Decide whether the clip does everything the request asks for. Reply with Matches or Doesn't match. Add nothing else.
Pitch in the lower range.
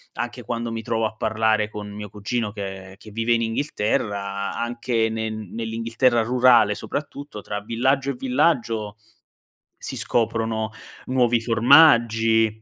Matches